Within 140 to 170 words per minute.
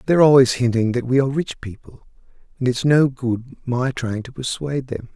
No: average, 200 wpm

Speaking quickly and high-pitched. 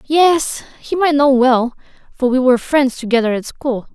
No: average, 180 wpm; very high, 265 Hz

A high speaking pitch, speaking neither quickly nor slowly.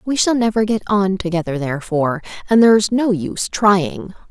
Yes: high, 195 Hz; average, 165 wpm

